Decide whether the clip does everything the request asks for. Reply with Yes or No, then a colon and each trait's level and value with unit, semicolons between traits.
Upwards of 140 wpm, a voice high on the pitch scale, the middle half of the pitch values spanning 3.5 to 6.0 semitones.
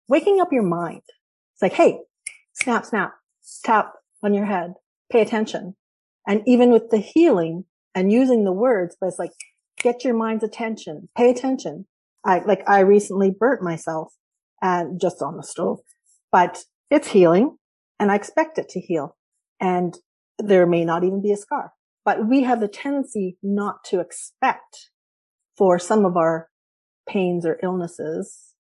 Yes: average, 160 wpm; high, 200 Hz; average, 5.1 semitones